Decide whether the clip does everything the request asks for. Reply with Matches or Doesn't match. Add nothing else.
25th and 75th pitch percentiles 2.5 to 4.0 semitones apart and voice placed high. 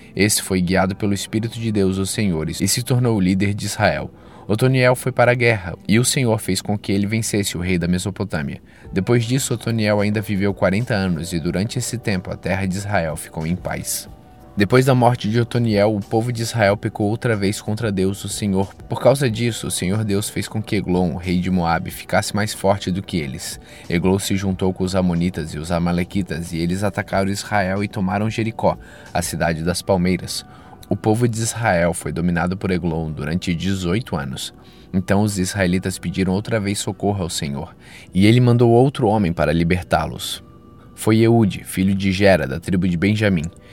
Doesn't match